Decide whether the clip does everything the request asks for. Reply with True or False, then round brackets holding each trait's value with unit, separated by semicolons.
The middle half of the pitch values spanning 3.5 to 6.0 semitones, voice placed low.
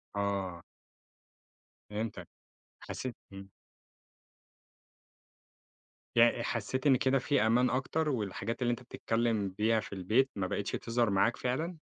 True (4.1 semitones; 115 Hz)